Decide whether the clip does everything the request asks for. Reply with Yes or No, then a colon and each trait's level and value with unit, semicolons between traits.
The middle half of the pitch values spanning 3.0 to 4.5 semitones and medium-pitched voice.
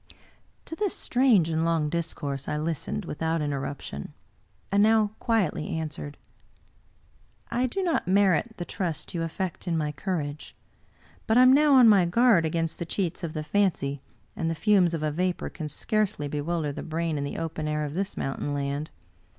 No: average, 5.0 semitones; medium, 165 Hz